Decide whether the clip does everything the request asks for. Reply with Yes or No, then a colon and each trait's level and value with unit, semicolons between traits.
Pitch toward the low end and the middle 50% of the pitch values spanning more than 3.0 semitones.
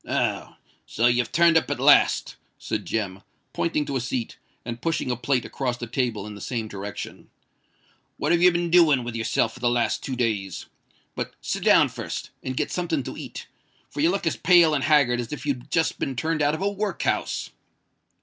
Yes: low, 130 Hz; wide, 5.4 semitones